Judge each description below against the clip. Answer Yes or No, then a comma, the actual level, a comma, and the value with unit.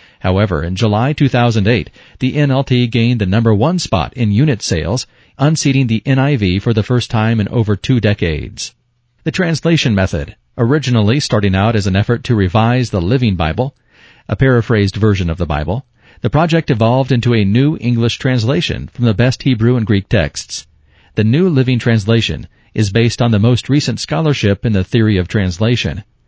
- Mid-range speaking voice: No, low, 115 Hz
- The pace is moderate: Yes, average, 175 wpm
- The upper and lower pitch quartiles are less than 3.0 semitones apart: No, average, 4.0 semitones